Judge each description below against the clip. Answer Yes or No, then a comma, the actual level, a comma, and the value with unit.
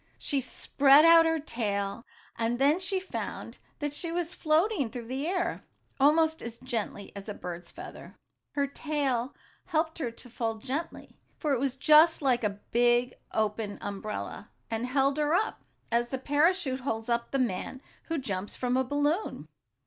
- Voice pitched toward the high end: Yes, very high, 265 Hz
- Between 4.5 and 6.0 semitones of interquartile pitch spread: Yes, average, 5.0 semitones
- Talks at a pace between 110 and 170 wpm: Yes, average, 165 wpm